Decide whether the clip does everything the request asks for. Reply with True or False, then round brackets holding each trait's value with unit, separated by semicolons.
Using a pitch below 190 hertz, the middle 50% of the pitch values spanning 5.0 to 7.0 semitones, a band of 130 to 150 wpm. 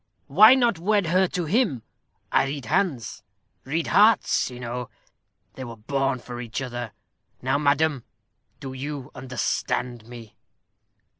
True (135 Hz; 5.3 semitones; 135 wpm)